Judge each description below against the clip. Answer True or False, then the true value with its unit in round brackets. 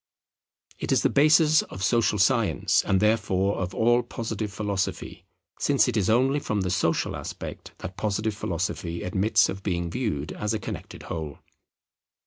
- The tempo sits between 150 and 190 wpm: True (155 wpm)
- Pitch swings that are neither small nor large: True (3.4 semitones)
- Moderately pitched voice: False (105 Hz)